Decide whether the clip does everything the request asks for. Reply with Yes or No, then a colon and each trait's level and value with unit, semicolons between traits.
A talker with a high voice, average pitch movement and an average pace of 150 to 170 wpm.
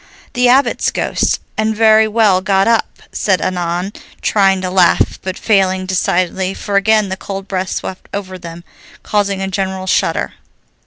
No: high, 195 Hz; narrow, 1.9 semitones; average, 155 wpm